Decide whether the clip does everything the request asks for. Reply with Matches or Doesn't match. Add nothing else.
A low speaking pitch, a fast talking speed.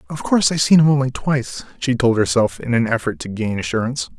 Matches